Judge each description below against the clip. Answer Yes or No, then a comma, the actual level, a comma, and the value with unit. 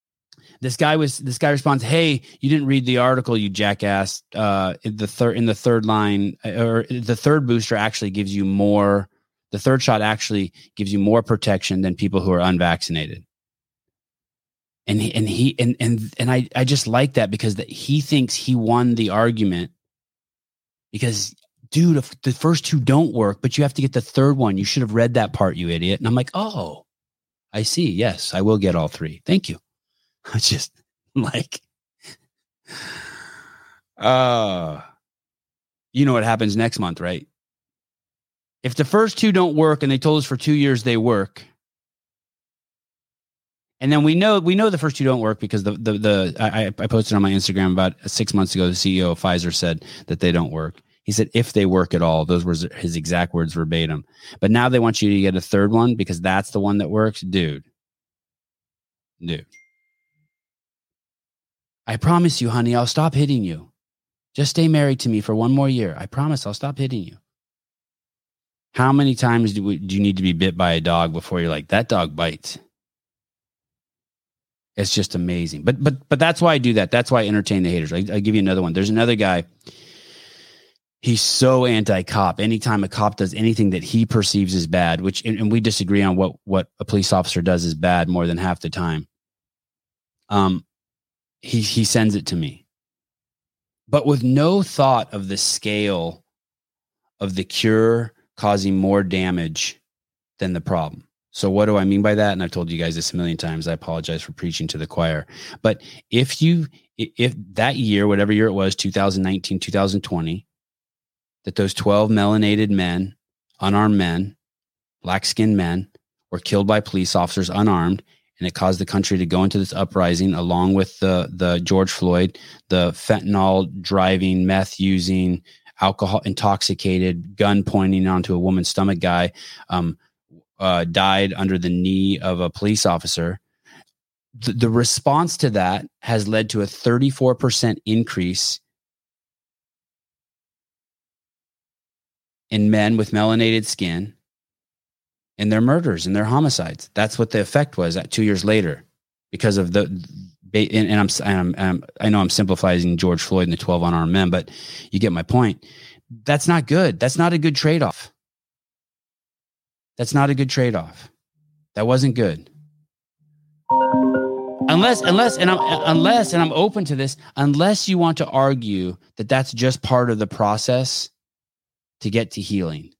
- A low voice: Yes, low, 105 Hz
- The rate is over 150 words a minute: Yes, average, 175 wpm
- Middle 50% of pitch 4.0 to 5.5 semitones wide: Yes, average, 5.2 semitones